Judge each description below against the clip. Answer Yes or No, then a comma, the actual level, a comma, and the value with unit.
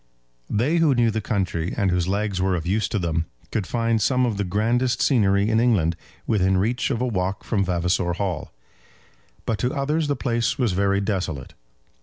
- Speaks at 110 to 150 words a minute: No, average, 190 wpm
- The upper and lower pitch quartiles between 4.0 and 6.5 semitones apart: Yes, average, 4.3 semitones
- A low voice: Yes, low, 100 Hz